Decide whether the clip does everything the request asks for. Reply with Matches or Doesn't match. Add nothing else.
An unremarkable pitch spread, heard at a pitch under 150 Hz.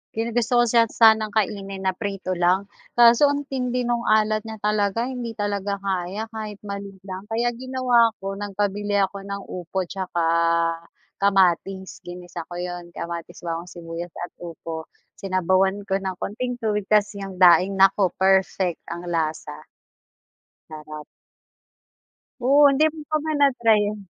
Doesn't match